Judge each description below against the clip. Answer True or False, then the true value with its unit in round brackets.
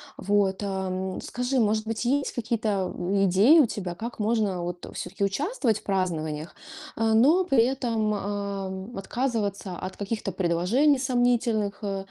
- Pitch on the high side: True (205 Hz)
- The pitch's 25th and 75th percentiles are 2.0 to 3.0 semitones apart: False (3.7 semitones)